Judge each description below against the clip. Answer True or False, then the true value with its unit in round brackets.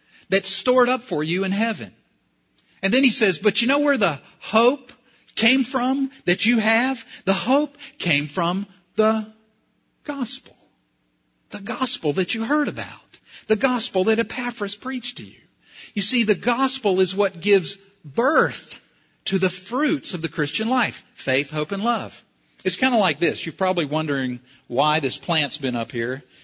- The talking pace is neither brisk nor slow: True (170 wpm)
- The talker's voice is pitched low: False (205 Hz)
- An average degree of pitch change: False (6.6 semitones)